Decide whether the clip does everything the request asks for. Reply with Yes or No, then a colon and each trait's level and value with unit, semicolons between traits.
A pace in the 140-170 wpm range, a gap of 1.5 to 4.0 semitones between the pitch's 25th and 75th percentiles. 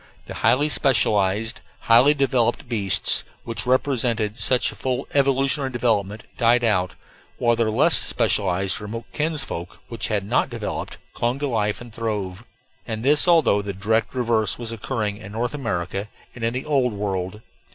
Yes: average, 155 wpm; average, 3.6 semitones